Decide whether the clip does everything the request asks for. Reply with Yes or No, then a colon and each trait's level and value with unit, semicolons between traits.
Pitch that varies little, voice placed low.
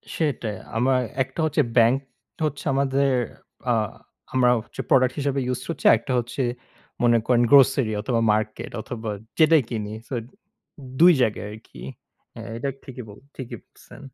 No: average, 3.1 semitones; low, 125 Hz